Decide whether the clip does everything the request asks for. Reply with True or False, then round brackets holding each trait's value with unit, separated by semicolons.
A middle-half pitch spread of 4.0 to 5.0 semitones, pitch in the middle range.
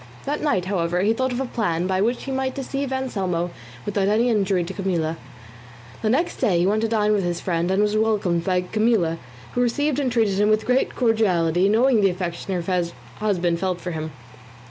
False (4.6 semitones; 200 Hz)